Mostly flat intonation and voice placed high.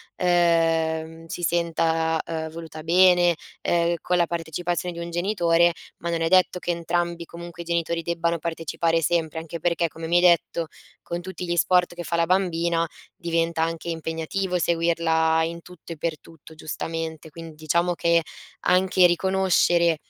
No: narrow, 1.1 semitones; medium, 170 Hz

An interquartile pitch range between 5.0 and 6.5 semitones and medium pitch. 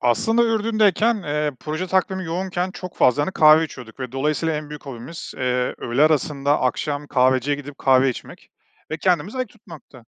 Yes: wide, 5.4 semitones; medium, 150 Hz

